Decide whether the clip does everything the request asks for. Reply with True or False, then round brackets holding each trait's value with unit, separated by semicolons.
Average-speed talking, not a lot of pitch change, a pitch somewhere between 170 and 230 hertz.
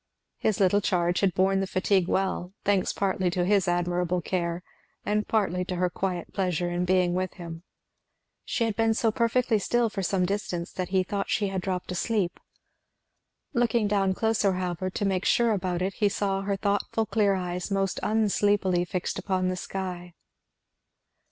True (170 wpm; 2.2 semitones; 190 Hz)